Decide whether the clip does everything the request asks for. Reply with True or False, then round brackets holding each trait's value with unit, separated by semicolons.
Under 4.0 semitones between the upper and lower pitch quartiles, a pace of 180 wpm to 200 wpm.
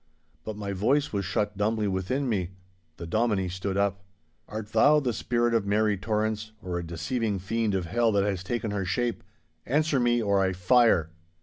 True (3.5 semitones; 185 wpm)